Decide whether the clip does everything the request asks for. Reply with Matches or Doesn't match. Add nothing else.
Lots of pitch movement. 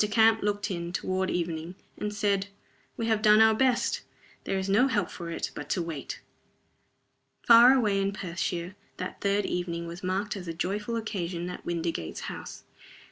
Doesn't match